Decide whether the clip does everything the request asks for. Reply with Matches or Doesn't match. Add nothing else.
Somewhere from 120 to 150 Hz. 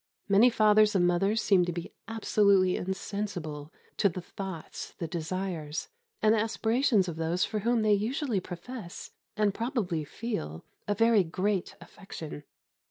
Doesn't match